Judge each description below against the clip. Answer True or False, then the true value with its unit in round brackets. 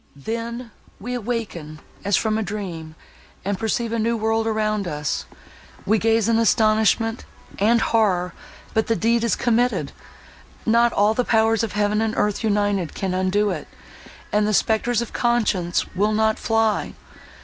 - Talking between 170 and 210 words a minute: False (145 wpm)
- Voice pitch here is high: True (220 Hz)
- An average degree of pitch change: False (1.9 semitones)